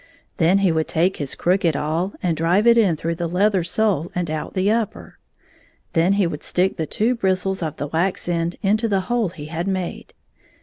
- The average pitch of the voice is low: No, medium, 180 Hz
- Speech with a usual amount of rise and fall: Yes, average, 3.1 semitones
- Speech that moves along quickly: Yes, fast, 210 wpm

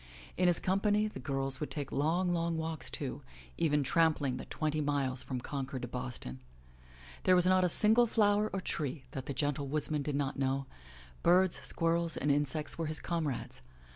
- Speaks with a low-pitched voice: No, medium, 155 Hz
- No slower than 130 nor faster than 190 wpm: Yes, average, 180 wpm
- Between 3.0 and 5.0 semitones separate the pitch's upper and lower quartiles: Yes, average, 4.2 semitones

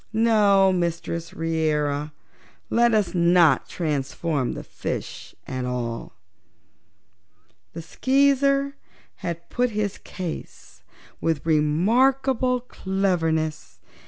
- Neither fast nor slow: No, slow, 85 wpm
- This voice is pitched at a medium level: Yes, medium, 170 Hz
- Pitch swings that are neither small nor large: No, wide, 6.3 semitones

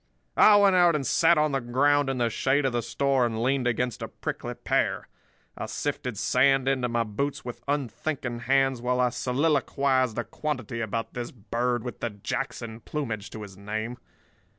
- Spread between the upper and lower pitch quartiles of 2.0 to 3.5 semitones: Yes, average, 2.9 semitones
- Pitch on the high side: No, low, 125 Hz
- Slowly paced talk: No, average, 180 wpm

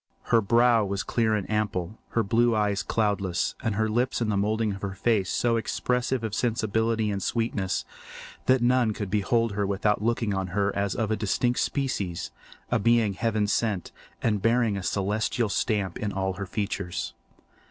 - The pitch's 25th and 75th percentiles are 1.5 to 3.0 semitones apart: Yes, narrow, 2.6 semitones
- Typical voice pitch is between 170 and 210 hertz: No, low, 105 Hz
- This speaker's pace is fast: No, average, 175 wpm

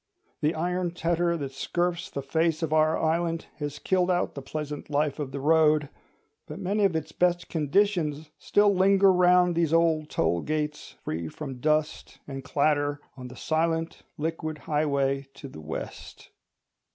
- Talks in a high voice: No, medium, 155 Hz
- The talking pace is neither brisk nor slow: Yes, average, 160 wpm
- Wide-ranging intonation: No, average, 3.0 semitones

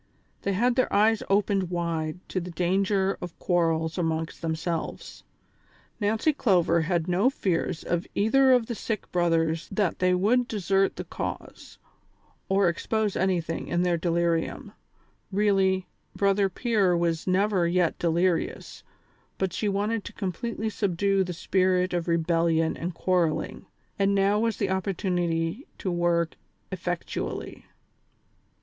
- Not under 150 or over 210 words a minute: No, average, 140 wpm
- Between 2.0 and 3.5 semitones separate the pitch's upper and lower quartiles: Yes, average, 2.9 semitones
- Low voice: No, medium, 185 Hz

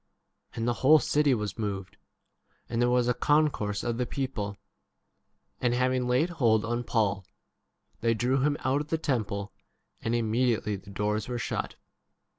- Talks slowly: No, average, 170 wpm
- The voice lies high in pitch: No, low, 120 Hz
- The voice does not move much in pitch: No, average, 3.4 semitones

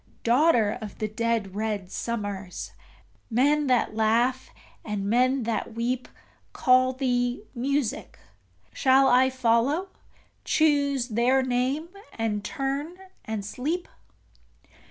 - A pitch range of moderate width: Yes, average, 3.4 semitones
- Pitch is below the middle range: No, high, 245 Hz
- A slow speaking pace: Yes, slow, 105 wpm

